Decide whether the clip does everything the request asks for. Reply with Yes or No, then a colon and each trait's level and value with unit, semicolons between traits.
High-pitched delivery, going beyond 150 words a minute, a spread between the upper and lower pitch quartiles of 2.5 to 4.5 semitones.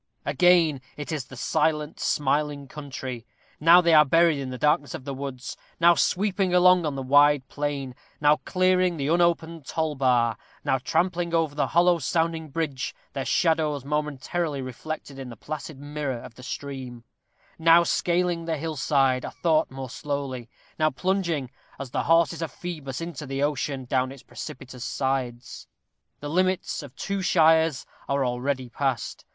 No: medium, 150 Hz; average, 160 wpm; average, 3.8 semitones